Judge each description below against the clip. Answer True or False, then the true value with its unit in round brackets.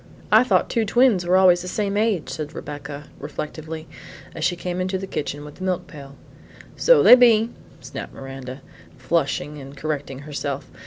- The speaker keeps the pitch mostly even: False (5.0 semitones)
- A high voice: False (165 Hz)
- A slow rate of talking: False (170 wpm)